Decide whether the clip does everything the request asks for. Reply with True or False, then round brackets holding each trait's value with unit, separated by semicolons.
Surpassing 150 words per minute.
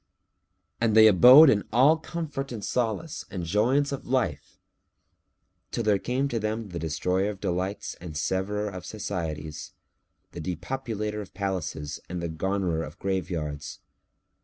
False (140 wpm)